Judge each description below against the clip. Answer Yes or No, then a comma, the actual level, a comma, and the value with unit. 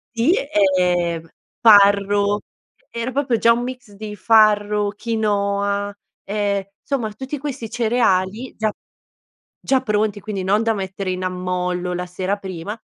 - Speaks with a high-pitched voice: Yes, high, 205 Hz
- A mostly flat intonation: No, average, 3.0 semitones